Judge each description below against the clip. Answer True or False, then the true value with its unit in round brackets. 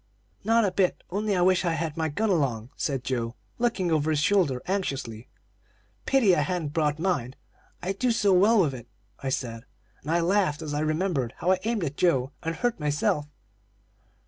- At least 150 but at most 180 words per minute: False (190 wpm)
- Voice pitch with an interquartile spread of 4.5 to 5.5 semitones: True (5.2 semitones)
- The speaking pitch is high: False (165 Hz)